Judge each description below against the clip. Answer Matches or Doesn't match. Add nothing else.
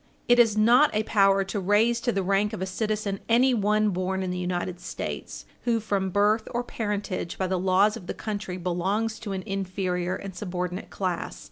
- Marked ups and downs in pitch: Doesn't match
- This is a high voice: Matches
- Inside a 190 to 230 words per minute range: Matches